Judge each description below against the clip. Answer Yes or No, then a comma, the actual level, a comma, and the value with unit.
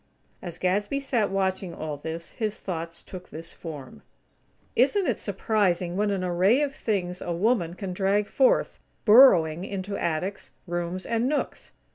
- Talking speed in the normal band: Yes, average, 150 wpm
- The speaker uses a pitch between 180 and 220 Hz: Yes, high, 190 Hz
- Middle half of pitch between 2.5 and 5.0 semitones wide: Yes, average, 3.6 semitones